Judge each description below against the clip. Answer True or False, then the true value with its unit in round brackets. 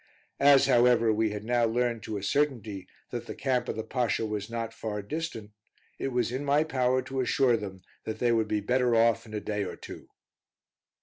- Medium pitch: False (115 Hz)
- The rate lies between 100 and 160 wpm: False (205 wpm)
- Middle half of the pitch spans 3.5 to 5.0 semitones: False (2.8 semitones)